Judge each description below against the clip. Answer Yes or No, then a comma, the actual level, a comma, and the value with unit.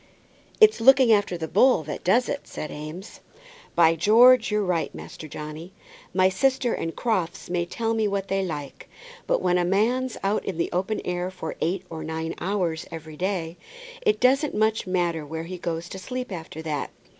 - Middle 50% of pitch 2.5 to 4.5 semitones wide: No, average, 5.1 semitones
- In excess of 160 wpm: Yes, average, 185 wpm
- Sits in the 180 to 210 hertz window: Yes, medium, 185 Hz